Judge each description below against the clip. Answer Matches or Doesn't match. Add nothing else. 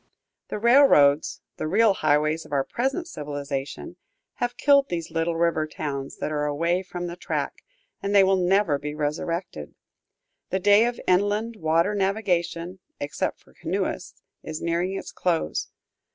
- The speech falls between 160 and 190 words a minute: Doesn't match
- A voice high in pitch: Doesn't match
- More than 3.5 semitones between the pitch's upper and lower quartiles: Matches